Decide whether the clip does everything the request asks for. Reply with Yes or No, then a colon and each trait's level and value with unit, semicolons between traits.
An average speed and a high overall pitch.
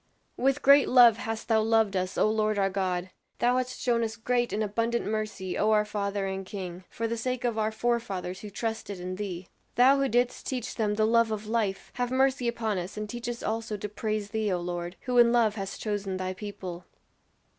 No: fast, 215 wpm; high, 215 Hz